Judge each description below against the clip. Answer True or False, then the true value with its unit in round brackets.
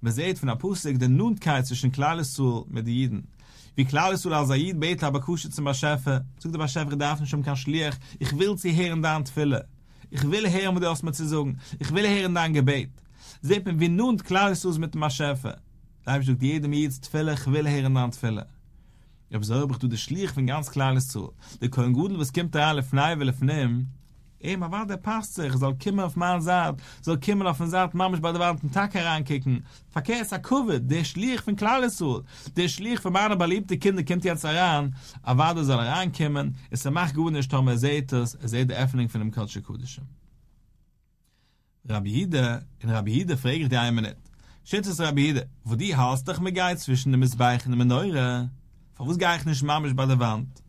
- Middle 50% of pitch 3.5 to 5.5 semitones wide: True (5.0 semitones)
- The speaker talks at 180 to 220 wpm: True (200 wpm)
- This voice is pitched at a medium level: True (145 Hz)